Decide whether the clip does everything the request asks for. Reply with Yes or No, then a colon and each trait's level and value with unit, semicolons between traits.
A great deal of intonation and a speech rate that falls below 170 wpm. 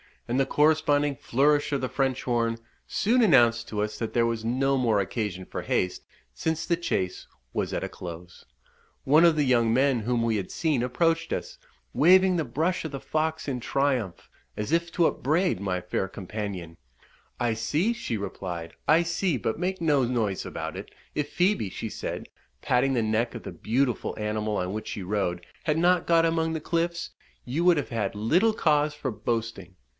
No: wide, 6.9 semitones; average, 190 wpm